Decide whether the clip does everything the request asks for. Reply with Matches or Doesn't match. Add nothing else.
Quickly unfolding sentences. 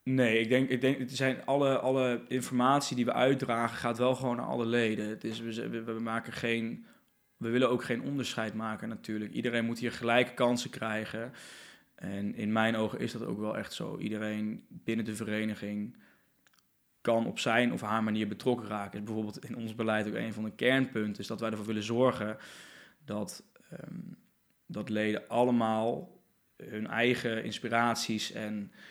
Doesn't match